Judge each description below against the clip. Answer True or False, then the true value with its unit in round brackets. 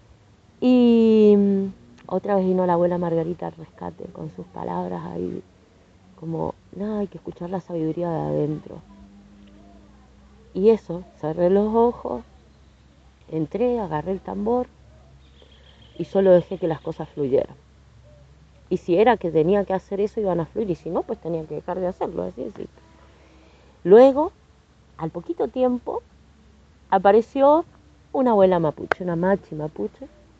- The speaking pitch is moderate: True (170 Hz)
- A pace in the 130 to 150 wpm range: True (140 wpm)